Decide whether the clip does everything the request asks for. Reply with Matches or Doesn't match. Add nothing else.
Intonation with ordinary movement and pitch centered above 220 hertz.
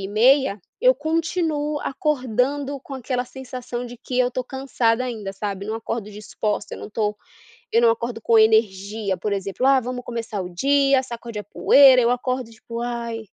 Matches